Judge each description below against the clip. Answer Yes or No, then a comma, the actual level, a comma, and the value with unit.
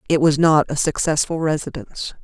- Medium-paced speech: Yes, average, 160 wpm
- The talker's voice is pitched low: No, medium, 150 Hz